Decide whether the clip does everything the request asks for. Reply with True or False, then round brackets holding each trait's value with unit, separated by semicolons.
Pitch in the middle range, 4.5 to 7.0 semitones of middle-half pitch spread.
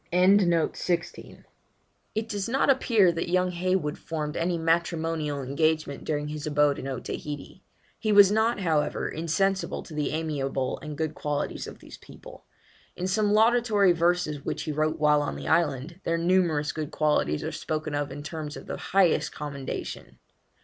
False (160 Hz; 3.6 semitones)